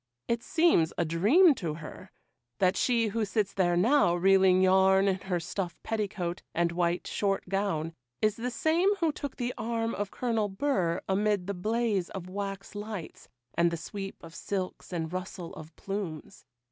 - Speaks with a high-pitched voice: Yes, high, 195 Hz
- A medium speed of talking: Yes, average, 170 wpm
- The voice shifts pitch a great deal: No, average, 4.1 semitones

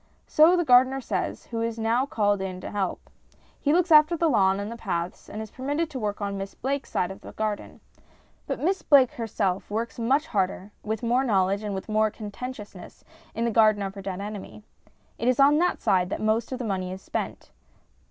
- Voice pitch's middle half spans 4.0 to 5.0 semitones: Yes, average, 4.6 semitones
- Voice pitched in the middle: No, high, 220 Hz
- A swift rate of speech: Yes, fast, 210 wpm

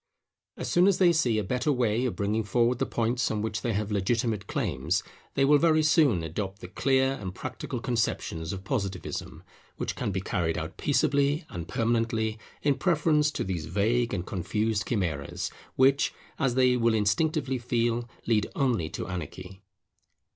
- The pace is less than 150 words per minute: No, average, 170 wpm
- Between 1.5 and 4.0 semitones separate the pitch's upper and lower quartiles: No, average, 5.1 semitones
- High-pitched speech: No, low, 115 Hz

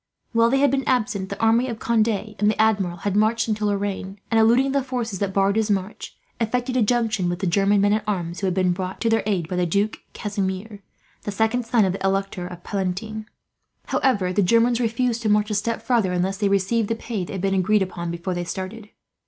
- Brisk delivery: Yes, fast, 225 wpm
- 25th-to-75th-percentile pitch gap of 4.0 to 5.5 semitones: No, average, 3.0 semitones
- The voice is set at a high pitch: Yes, high, 210 Hz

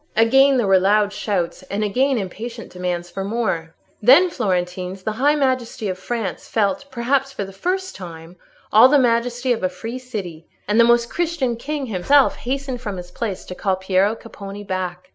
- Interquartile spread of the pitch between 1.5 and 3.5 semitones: No, average, 5.2 semitones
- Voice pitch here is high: Yes, high, 215 Hz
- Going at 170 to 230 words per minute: Yes, average, 180 wpm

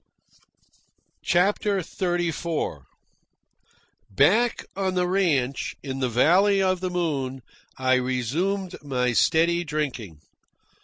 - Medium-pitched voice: Yes, medium, 170 Hz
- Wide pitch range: Yes, wide, 6.2 semitones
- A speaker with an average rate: No, slow, 95 wpm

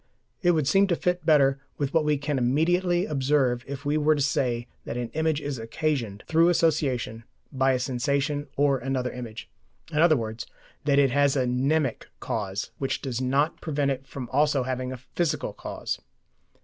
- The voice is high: No, medium, 140 Hz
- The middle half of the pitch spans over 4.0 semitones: No, average, 3.1 semitones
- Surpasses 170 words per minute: Yes, average, 180 wpm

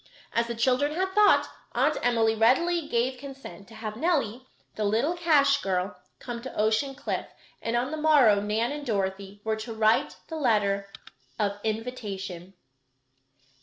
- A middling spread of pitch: Yes, average, 4.9 semitones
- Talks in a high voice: Yes, high, 230 Hz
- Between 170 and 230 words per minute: No, average, 155 wpm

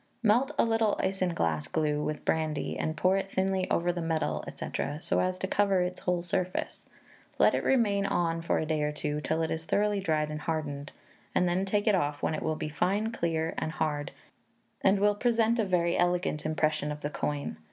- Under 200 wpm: No, fast, 205 wpm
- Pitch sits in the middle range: Yes, medium, 170 Hz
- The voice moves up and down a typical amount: Yes, average, 4.0 semitones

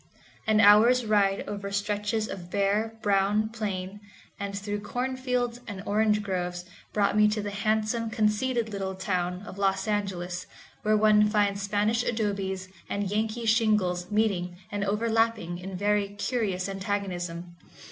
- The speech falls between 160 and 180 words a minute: No, slow, 135 wpm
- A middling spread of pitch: No, narrow, 1.9 semitones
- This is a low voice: No, high, 205 Hz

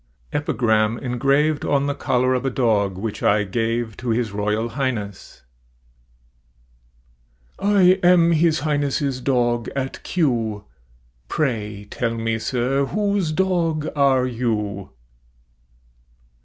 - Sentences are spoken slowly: Yes, slow, 110 wpm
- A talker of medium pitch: No, low, 125 Hz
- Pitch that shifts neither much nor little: Yes, average, 4.5 semitones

